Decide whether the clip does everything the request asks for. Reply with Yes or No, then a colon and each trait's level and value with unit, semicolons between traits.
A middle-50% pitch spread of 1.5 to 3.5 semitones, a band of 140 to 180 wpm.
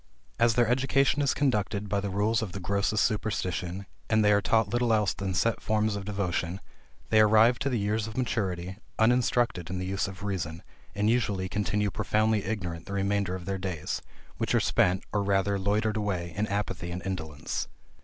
No: average, 2.7 semitones; average, 190 wpm